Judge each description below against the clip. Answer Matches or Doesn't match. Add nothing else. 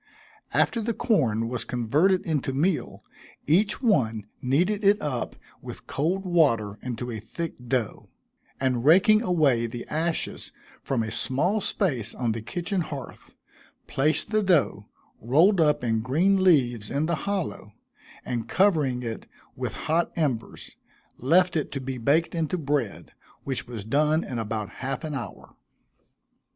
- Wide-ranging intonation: Matches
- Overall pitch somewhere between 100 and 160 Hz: Matches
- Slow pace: Doesn't match